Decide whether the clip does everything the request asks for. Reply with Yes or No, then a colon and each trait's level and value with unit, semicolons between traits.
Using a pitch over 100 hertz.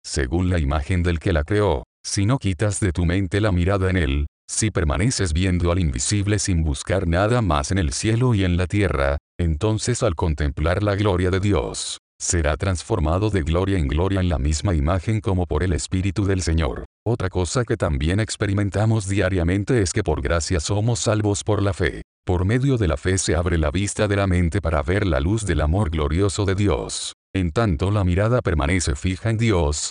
No: very low, 95 Hz